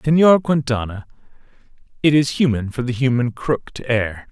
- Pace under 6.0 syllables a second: Yes, 5.0 syllables/s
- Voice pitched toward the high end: No, low, 130 Hz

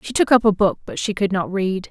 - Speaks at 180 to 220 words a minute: No, fast, 315 wpm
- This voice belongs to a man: No, female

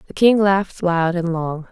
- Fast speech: Yes, fast, 210 wpm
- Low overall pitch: No, medium, 180 Hz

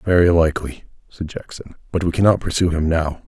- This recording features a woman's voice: No, male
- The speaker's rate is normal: Yes, average, 180 wpm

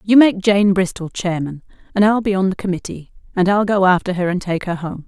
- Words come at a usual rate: No, fast, 235 wpm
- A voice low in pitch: No, high, 190 Hz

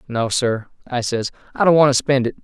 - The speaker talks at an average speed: No, fast, 245 wpm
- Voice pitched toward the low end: Yes, low, 130 Hz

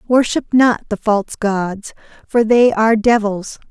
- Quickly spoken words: No, average, 145 wpm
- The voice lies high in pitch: Yes, high, 220 Hz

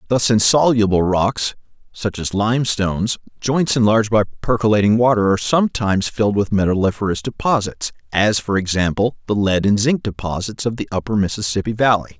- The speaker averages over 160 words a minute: No, average, 150 wpm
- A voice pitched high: No, low, 105 Hz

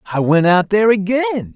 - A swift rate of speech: No, average, 195 wpm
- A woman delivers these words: No, male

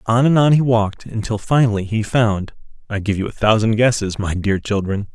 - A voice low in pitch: Yes, low, 110 Hz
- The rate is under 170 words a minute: No, average, 200 wpm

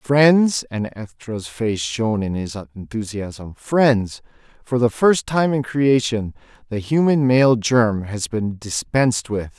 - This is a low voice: Yes, low, 115 Hz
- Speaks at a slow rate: Yes, slow, 130 wpm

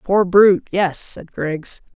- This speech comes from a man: No, female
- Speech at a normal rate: Yes, average, 150 wpm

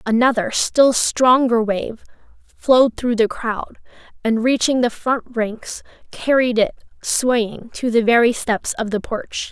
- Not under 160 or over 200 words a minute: No, average, 145 wpm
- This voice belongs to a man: No, female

